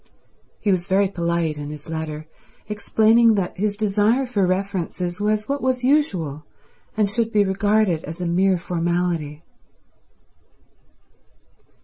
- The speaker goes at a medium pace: No, slow, 125 wpm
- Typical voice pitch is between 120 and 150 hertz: No, high, 190 Hz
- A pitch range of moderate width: Yes, average, 3.9 semitones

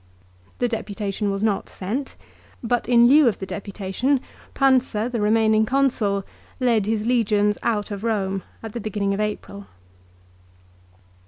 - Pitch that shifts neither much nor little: Yes, average, 3.0 semitones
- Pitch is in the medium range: No, high, 215 Hz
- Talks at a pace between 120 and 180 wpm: Yes, average, 140 wpm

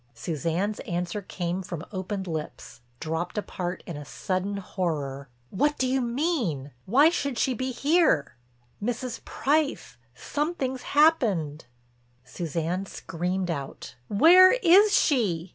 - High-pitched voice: Yes, high, 195 Hz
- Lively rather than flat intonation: Yes, wide, 8.0 semitones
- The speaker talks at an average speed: No, slow, 120 wpm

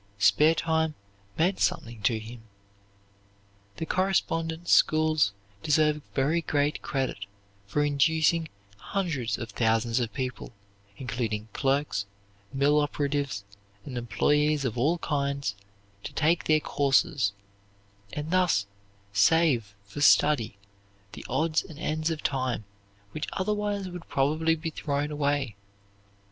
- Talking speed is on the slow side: Yes, slow, 115 wpm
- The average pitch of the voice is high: No, medium, 145 Hz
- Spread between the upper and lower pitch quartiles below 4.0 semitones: No, average, 4.6 semitones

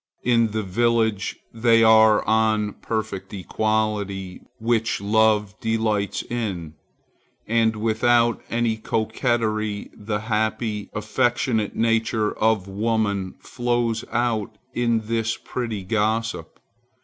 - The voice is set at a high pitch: No, low, 110 Hz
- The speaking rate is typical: No, slow, 100 wpm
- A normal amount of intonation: No, narrow, 1.4 semitones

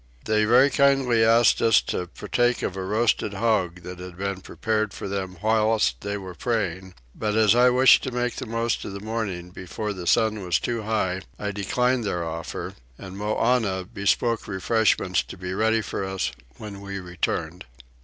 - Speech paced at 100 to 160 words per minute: No, average, 180 wpm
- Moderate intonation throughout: Yes, average, 3.4 semitones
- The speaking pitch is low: Yes, low, 105 Hz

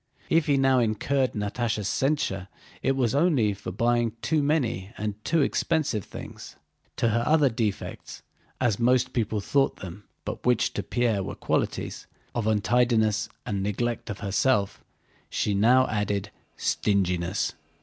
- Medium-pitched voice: No, low, 115 Hz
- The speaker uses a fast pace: No, average, 140 wpm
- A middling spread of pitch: Yes, average, 4.0 semitones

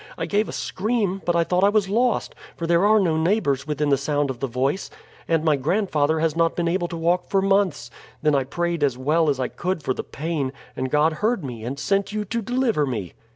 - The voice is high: No, medium, 165 Hz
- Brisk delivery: Yes, fast, 235 wpm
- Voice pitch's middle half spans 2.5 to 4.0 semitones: No, wide, 5.5 semitones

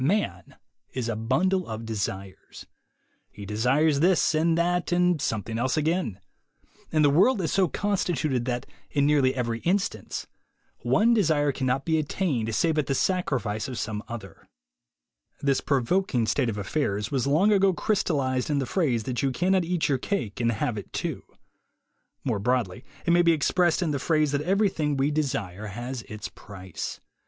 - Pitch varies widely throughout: Yes, wide, 6.5 semitones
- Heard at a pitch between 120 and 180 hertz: Yes, medium, 140 Hz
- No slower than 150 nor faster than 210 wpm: Yes, average, 165 wpm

